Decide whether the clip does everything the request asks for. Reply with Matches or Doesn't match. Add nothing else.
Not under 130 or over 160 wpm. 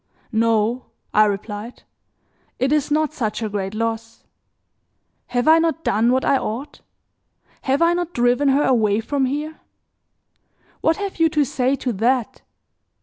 Matches